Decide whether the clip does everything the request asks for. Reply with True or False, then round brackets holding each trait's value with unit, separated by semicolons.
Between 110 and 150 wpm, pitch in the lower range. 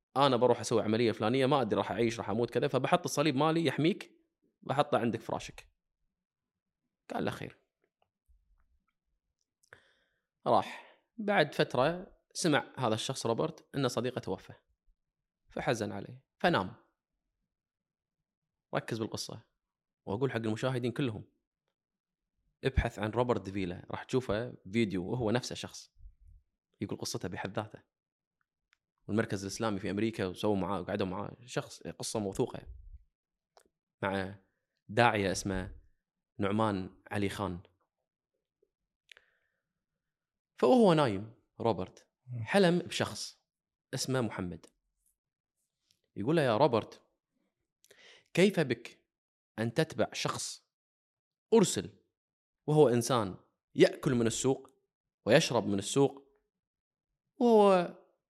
False (100 wpm; 115 Hz)